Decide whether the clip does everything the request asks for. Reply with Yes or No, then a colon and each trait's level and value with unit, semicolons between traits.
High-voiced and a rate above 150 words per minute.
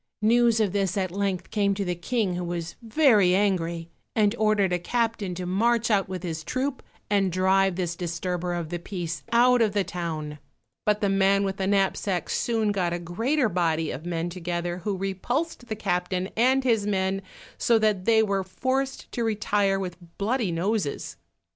Yes: high, 195 Hz; average, 180 wpm